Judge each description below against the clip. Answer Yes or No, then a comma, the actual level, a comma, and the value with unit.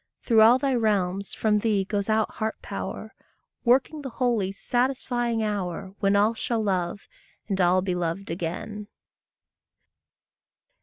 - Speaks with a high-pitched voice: Yes, high, 210 Hz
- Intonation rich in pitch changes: No, average, 3.3 semitones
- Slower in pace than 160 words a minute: Yes, slow, 135 wpm